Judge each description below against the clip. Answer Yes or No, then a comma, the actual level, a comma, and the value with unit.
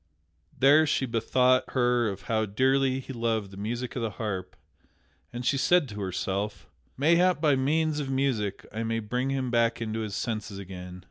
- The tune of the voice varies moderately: Yes, average, 4.0 semitones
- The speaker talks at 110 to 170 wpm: No, average, 180 wpm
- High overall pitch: No, low, 120 Hz